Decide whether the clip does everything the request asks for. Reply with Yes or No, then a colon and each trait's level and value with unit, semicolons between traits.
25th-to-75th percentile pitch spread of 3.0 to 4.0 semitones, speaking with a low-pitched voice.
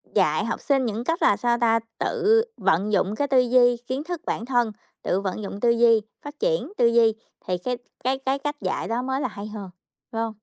No: average, 3.7 semitones; high, 240 Hz